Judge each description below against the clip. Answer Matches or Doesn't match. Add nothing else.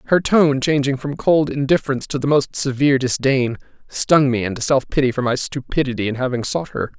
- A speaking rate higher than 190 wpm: Matches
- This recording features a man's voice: Matches